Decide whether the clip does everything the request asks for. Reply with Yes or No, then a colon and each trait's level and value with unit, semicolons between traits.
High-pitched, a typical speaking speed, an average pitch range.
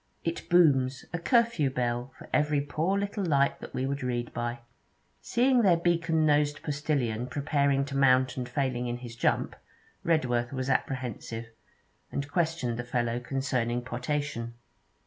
No: low, 135 Hz; average, 145 wpm; average, 4.0 semitones